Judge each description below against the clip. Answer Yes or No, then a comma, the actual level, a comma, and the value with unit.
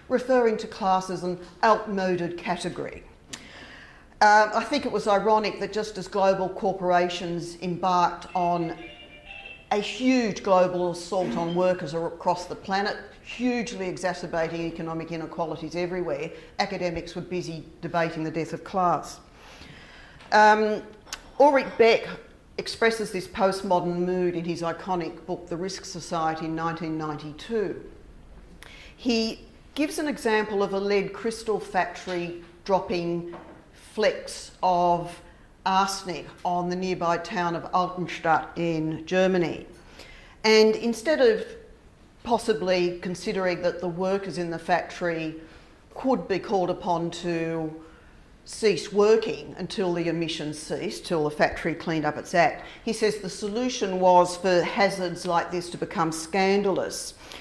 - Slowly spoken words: Yes, slow, 125 wpm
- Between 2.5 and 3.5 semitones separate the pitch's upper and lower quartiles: Yes, average, 3.2 semitones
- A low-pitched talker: No, medium, 180 Hz